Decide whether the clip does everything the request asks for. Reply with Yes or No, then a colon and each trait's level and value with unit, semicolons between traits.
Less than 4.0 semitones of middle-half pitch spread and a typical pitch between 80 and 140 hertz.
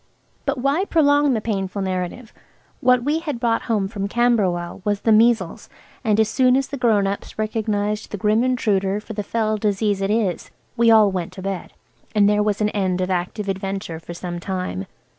No: average, 3.3 semitones; high, 210 Hz